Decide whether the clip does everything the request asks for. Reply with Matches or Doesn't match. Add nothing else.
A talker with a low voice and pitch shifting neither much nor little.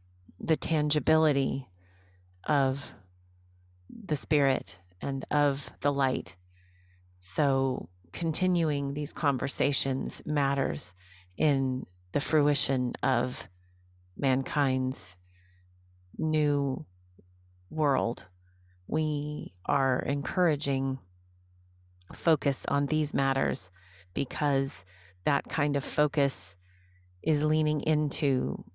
Doesn't match